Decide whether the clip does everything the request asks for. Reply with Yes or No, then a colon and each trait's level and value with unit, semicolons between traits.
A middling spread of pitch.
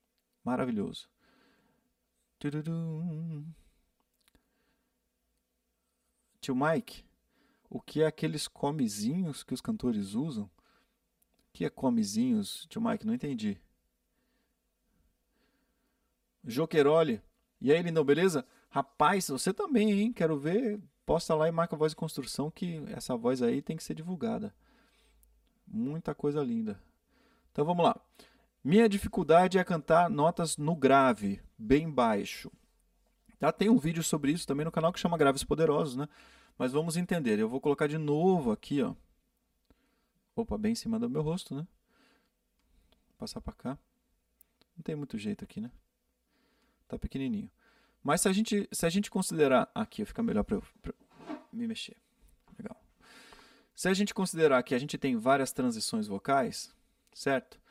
No: wide, 6.5 semitones